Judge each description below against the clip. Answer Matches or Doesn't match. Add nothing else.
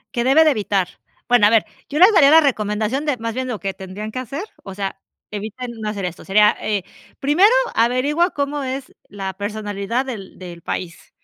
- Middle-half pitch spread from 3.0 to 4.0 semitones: Doesn't match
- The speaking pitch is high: Matches